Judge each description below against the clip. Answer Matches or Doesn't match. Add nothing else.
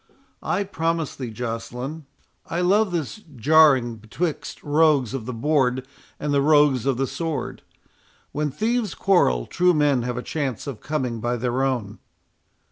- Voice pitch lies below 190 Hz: Matches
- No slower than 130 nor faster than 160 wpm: Matches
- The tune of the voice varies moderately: Matches